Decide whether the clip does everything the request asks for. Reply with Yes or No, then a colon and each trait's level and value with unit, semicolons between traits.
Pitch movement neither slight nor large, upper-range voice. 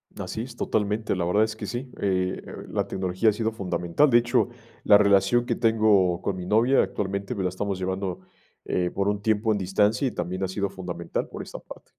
No: average, 3.0 semitones; low, 100 Hz